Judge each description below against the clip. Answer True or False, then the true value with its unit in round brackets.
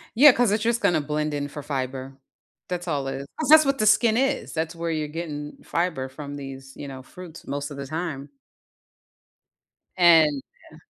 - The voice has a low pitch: False (155 Hz)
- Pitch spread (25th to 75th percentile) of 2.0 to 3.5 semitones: False (4.4 semitones)